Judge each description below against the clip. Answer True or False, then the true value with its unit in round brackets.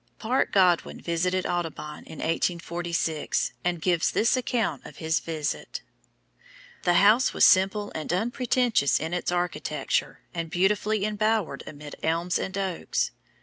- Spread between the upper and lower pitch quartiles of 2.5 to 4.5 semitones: True (4.0 semitones)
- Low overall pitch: False (180 Hz)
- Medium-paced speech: False (130 wpm)